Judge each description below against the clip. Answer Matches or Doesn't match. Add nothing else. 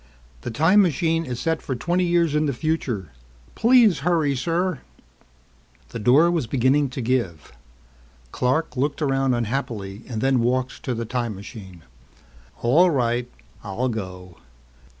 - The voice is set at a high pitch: Doesn't match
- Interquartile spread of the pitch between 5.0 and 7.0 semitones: Matches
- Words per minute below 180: Matches